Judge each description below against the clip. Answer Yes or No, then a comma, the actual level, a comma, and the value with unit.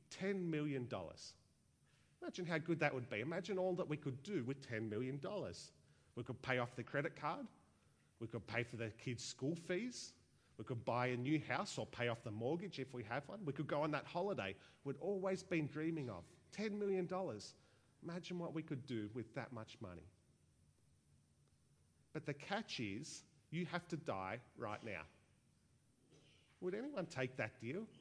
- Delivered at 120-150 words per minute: No, average, 180 wpm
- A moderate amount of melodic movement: No, wide, 6.4 semitones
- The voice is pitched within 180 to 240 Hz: No, low, 135 Hz